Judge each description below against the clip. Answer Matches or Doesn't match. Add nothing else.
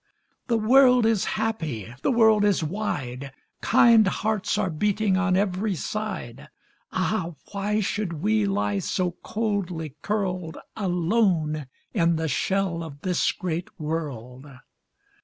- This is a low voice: Doesn't match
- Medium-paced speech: Doesn't match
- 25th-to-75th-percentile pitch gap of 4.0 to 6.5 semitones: Matches